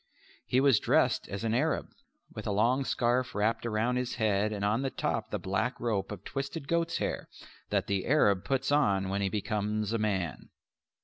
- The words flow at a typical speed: Yes, average, 190 wpm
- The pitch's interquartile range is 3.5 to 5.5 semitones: Yes, average, 4.2 semitones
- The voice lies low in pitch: Yes, low, 110 Hz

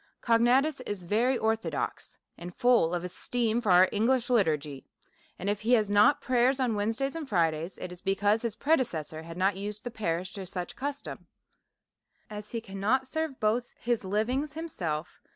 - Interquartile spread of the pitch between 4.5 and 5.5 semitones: Yes, average, 5.1 semitones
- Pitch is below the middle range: No, high, 215 Hz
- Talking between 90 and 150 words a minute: No, average, 175 wpm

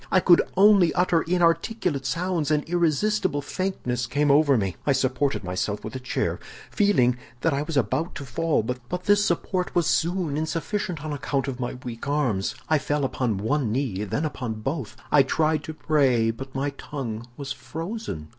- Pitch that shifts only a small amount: No, average, 4.8 semitones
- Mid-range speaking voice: Yes, medium, 145 Hz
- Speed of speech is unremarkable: Yes, average, 175 wpm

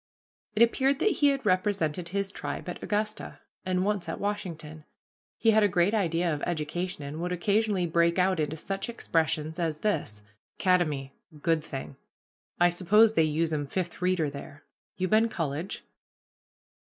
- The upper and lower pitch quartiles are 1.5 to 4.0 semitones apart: No, average, 4.5 semitones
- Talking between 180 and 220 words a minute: No, average, 155 wpm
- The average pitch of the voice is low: No, medium, 175 Hz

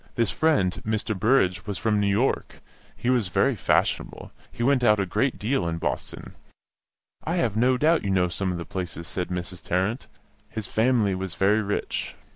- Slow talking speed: No, average, 185 wpm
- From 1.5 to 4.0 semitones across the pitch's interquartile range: No, average, 4.7 semitones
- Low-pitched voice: Yes, low, 105 Hz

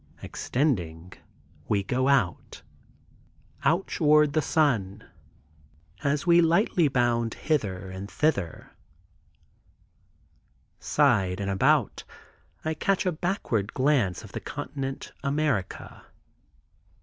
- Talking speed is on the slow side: Yes, slow, 95 wpm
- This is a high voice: No, low, 135 Hz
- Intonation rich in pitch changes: Yes, wide, 7.7 semitones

